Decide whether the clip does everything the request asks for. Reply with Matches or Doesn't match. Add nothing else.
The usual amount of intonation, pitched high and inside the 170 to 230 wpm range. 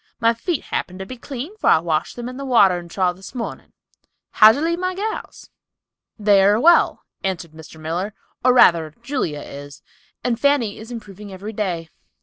Doesn't match